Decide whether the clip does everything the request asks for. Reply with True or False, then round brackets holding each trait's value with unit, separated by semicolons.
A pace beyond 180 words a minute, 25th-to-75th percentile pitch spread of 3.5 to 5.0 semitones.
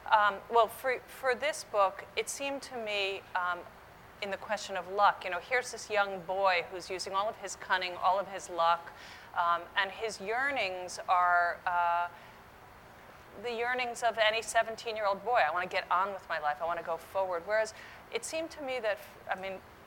True (200 wpm; 4.2 semitones)